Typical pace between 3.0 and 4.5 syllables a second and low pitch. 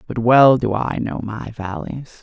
Yes: 4.0 syllables/s; low, 115 Hz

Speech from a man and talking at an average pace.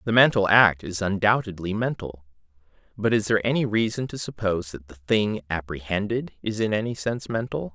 Yes: male; average, 170 wpm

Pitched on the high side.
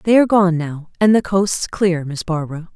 No: medium, 180 Hz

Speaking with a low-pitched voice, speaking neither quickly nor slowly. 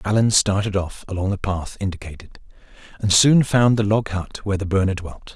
Yes: low, 100 Hz; average, 190 wpm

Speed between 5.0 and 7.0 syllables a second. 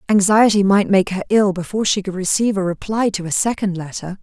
Yes: 6.1 syllables/s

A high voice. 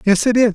Yes: high, 220 Hz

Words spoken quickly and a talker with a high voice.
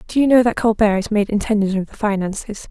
Yes: fast, 245 wpm; high, 210 Hz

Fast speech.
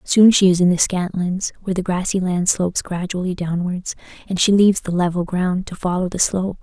Yes: fast, 210 wpm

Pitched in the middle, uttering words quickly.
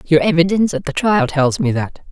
Yes: medium, 170 Hz; fast, 225 wpm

